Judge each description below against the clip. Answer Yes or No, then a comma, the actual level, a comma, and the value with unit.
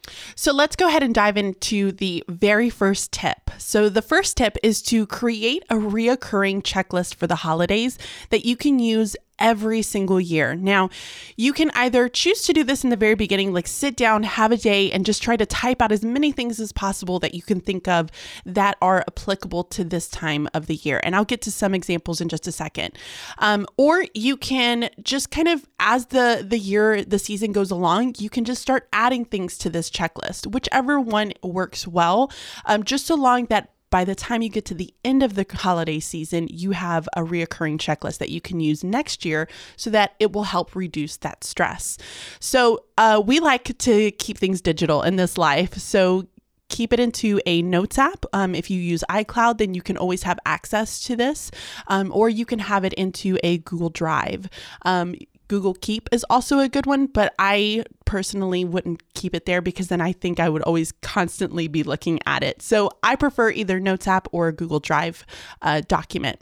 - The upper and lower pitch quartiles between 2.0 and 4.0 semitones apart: No, average, 4.8 semitones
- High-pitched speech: Yes, high, 200 Hz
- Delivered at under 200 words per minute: No, fast, 205 wpm